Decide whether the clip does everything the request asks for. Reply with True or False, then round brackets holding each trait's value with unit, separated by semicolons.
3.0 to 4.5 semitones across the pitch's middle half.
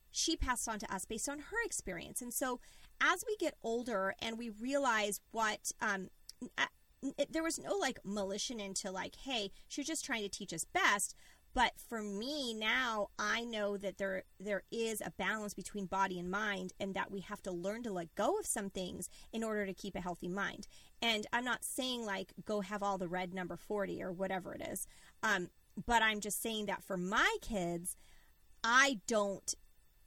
True (3.5 semitones)